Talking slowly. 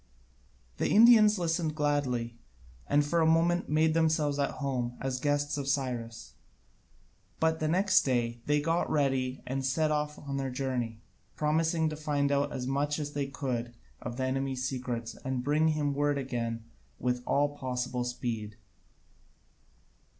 No: average, 155 wpm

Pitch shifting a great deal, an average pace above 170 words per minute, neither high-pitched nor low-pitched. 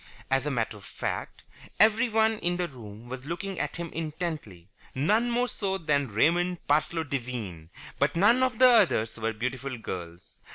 No: wide, 8.8 semitones; average, 165 wpm; medium, 150 Hz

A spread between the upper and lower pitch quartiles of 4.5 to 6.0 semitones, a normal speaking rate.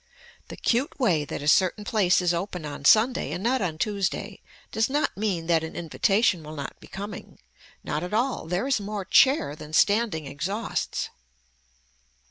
Yes: average, 5.3 semitones; average, 170 wpm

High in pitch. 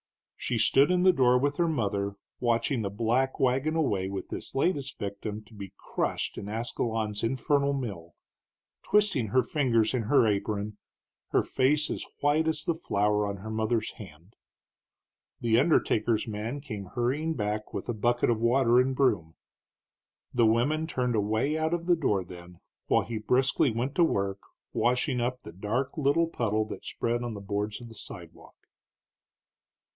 No: low, 120 Hz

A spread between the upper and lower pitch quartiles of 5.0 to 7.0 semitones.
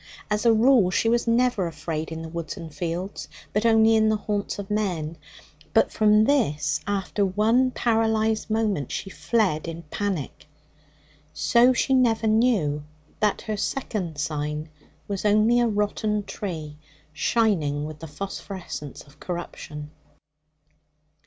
Yes: wide, 5.5 semitones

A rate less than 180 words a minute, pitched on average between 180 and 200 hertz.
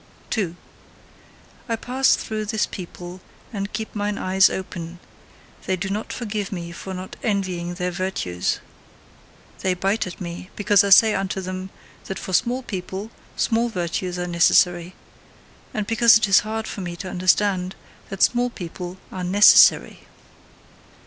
Yes: average, 150 wpm; high, 190 Hz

